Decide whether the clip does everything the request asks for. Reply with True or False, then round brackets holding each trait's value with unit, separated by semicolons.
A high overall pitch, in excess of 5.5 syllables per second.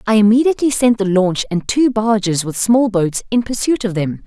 False (215 Hz; 5.2 syllables/s)